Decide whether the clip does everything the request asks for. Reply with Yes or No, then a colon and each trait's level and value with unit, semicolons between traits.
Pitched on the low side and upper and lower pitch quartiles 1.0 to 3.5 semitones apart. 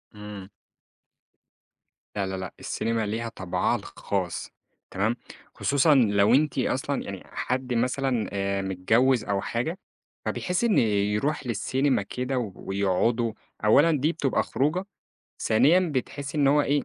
No: low, 120 Hz; wide, 5.5 semitones